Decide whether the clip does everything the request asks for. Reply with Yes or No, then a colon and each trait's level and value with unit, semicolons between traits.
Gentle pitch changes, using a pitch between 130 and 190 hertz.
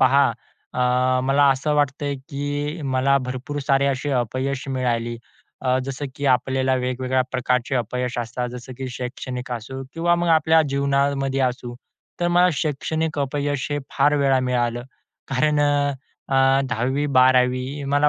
Yes: narrow, 2.1 semitones; low, 135 Hz